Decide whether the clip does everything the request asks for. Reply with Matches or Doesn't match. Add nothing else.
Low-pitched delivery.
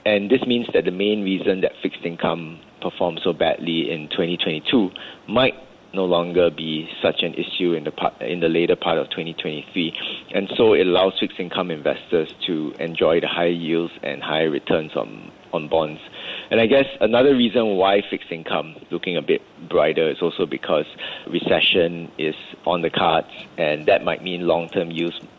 Matches